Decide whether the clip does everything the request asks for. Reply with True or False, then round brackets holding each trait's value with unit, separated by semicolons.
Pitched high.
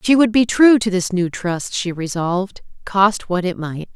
True (195 Hz)